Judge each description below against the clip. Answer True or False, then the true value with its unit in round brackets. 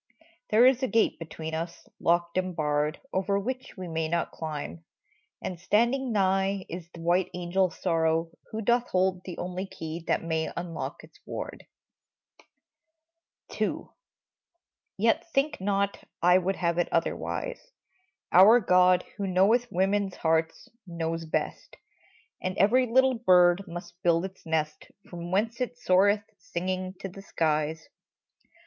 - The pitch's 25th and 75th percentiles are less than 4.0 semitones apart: True (3.2 semitones)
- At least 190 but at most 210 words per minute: False (140 wpm)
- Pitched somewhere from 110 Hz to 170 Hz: False (185 Hz)